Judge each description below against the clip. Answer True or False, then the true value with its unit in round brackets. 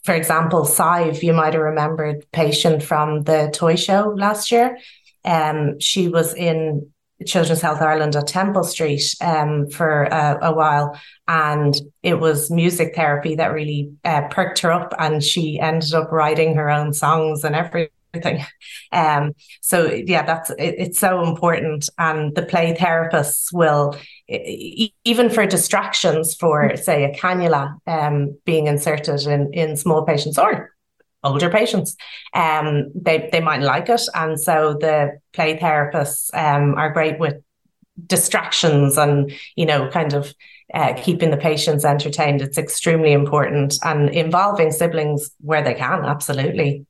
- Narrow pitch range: True (2.3 semitones)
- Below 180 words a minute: True (150 wpm)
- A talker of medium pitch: True (155 Hz)